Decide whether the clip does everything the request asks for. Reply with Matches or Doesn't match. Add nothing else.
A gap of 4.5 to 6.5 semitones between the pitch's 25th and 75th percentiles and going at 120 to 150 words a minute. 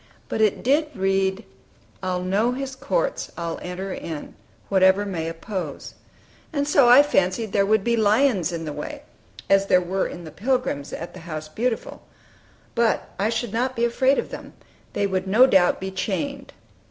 Doesn't match